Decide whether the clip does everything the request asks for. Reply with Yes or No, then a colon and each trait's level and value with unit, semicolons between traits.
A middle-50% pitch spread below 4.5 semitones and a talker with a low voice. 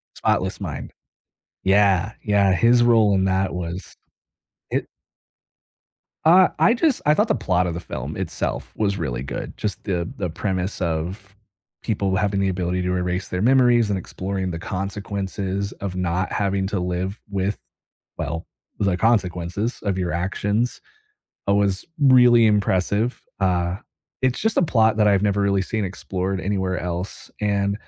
Yes: narrow, 2.4 semitones; low, 100 Hz